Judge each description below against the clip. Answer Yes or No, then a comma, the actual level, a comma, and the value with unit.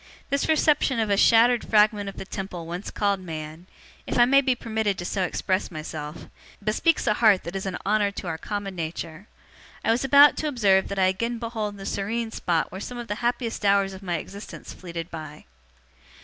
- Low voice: No, high, 200 Hz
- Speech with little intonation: No, average, 3.9 semitones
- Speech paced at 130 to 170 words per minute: No, fast, 205 wpm